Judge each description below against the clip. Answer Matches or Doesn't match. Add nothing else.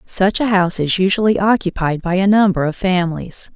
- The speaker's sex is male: Doesn't match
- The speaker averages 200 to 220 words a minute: Doesn't match